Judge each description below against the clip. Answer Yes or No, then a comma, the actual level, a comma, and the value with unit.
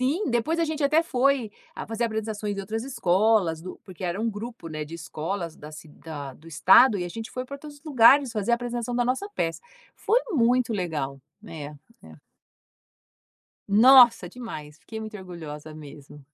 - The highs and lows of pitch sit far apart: Yes, wide, 7.0 semitones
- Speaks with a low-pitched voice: No, high, 215 Hz